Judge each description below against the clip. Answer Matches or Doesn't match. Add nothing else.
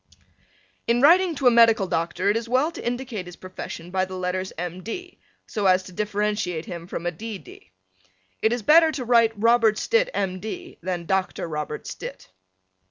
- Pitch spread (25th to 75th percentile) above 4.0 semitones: Matches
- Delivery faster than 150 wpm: Matches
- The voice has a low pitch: Doesn't match